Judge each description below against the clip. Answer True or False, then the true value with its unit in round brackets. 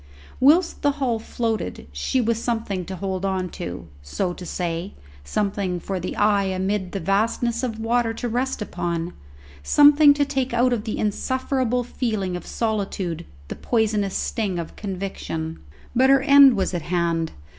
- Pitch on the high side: True (210 Hz)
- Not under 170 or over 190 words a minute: False (160 wpm)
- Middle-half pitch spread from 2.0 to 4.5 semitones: False (5.0 semitones)